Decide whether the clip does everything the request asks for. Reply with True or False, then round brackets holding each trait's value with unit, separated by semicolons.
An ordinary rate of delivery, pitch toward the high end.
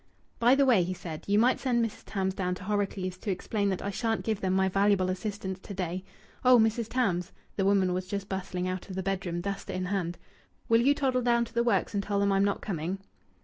False (235 wpm; 195 Hz)